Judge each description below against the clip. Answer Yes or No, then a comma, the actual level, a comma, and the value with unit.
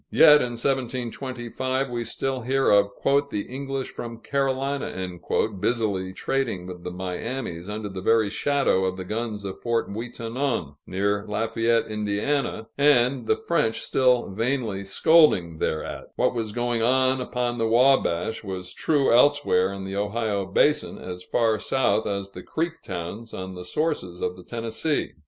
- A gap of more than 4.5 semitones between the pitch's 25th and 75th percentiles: Yes, average, 5.0 semitones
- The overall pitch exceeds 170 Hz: No, low, 115 Hz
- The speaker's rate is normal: Yes, average, 150 wpm